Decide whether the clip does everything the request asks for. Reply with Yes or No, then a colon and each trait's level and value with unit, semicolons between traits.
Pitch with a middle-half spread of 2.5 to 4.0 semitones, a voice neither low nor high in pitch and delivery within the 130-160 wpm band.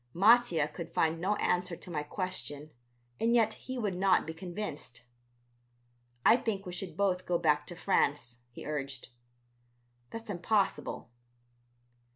No: average, 4.8 semitones; medium, 180 Hz; average, 140 wpm